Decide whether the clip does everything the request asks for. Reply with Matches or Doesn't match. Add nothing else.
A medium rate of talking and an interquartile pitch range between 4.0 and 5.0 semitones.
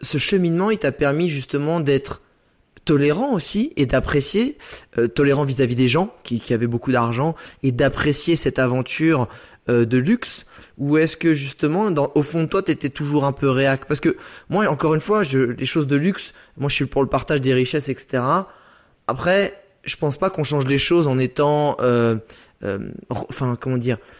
Doesn't match